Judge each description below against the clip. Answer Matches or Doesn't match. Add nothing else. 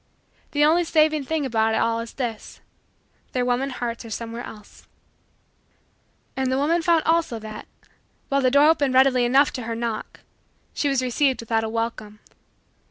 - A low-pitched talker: Doesn't match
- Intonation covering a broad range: Doesn't match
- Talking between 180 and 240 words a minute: Doesn't match